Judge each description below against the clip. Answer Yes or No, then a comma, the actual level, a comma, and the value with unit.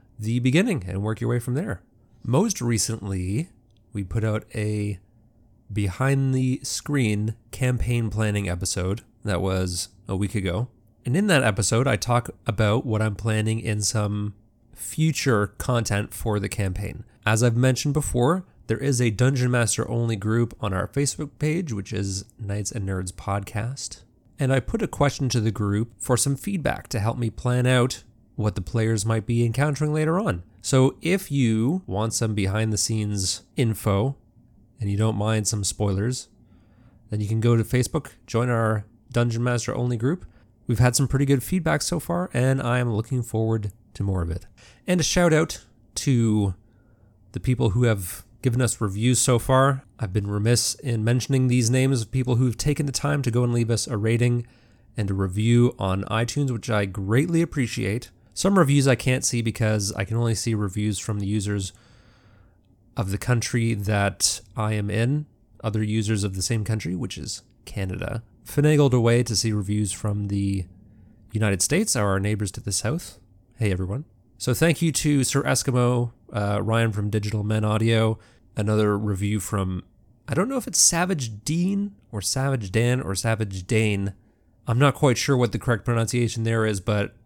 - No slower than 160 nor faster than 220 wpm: Yes, average, 175 wpm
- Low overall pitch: Yes, low, 115 Hz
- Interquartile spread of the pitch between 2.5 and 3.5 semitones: Yes, average, 3.2 semitones